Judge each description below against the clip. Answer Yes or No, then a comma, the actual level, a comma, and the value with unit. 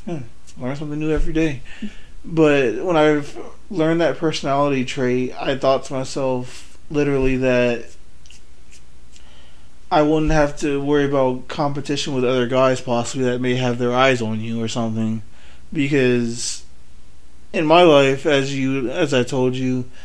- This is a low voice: Yes, low, 130 Hz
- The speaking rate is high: No, average, 145 wpm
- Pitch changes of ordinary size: Yes, average, 3.6 semitones